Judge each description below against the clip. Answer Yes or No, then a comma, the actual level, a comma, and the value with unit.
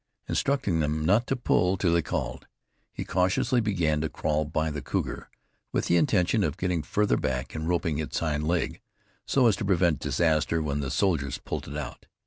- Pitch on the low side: Yes, very low, 80 Hz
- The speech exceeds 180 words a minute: Yes, average, 190 wpm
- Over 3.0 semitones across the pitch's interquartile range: Yes, average, 3.5 semitones